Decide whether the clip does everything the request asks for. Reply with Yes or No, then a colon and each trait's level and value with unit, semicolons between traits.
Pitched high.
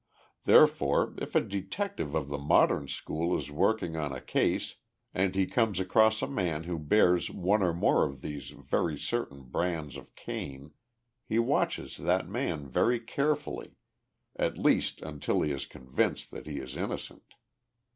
No: very low, 85 Hz